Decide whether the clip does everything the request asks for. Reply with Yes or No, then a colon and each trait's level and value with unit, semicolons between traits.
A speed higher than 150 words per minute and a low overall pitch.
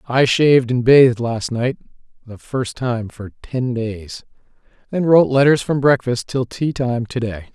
Yes: average, 175 wpm; low, 125 Hz